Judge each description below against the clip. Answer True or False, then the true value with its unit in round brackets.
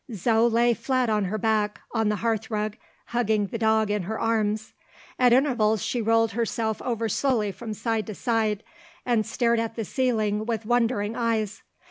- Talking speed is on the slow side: False (175 wpm)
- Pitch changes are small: True (1.7 semitones)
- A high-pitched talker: True (225 Hz)